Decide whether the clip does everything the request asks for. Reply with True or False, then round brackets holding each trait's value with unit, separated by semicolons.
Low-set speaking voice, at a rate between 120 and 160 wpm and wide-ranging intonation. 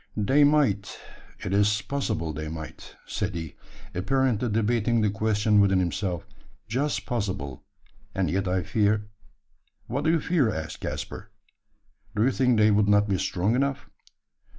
False (105 Hz; 150 wpm; 4.3 semitones)